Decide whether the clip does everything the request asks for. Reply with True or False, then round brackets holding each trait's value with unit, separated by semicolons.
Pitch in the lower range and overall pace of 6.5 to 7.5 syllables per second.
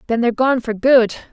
False (240 Hz; 7.0 syllables/s)